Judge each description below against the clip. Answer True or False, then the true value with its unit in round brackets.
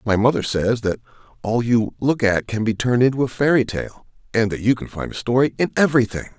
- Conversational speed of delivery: False (225 wpm)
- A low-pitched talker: True (120 Hz)